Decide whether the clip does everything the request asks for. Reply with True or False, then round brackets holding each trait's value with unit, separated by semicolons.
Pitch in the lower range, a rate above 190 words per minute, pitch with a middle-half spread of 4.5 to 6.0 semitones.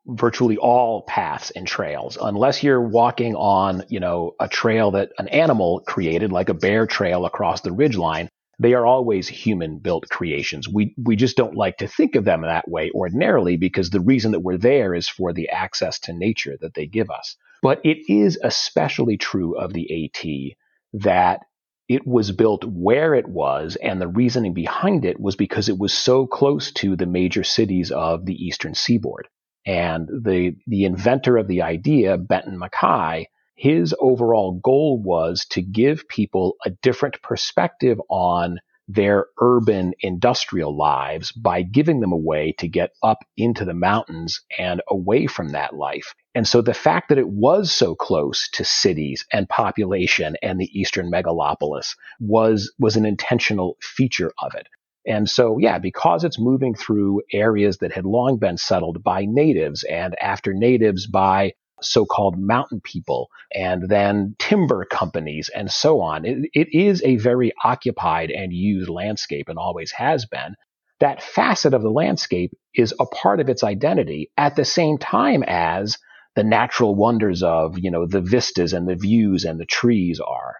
False (105 Hz; 170 wpm; 5.1 semitones)